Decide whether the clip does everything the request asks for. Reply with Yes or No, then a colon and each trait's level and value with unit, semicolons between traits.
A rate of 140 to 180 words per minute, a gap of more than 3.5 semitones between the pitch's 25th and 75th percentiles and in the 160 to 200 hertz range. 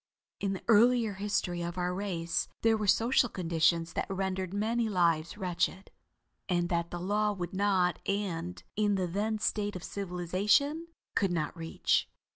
No: average, 155 wpm; average, 3.0 semitones; high, 190 Hz